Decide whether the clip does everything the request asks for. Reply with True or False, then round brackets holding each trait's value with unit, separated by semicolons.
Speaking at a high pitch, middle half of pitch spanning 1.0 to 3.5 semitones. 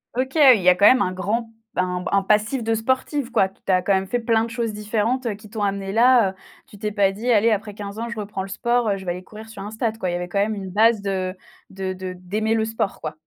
True (210 Hz; 2.9 semitones)